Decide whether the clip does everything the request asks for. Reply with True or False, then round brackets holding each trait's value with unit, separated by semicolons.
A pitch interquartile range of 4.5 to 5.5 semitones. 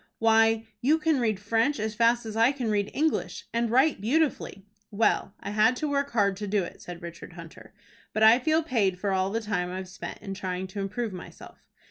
False (3.8 semitones)